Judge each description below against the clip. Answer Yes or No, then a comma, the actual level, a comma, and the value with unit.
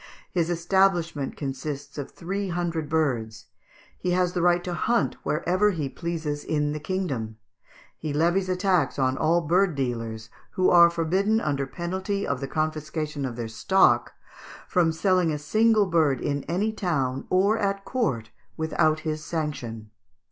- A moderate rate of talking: Yes, average, 155 wpm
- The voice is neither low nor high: Yes, medium, 160 Hz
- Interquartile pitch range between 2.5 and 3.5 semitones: No, average, 4.4 semitones